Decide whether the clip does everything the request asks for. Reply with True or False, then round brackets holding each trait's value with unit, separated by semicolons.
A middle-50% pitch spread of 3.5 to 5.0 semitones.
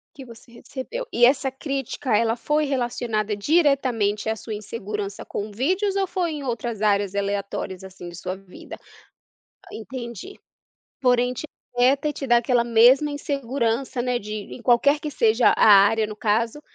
True (4.4 semitones)